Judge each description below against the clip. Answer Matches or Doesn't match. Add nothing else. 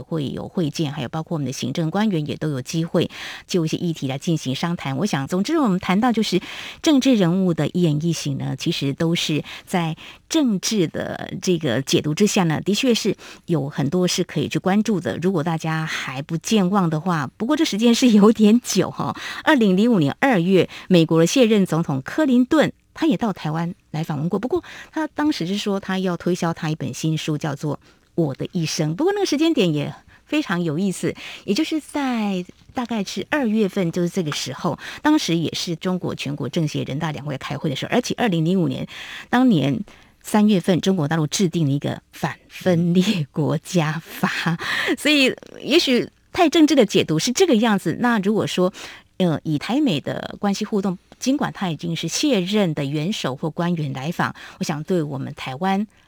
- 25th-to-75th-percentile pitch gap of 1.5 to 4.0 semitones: Doesn't match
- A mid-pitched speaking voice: Matches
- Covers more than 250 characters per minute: Matches